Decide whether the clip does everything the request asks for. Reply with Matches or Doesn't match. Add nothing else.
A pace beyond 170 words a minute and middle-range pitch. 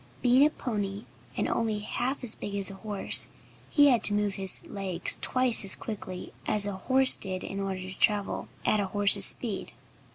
Doesn't match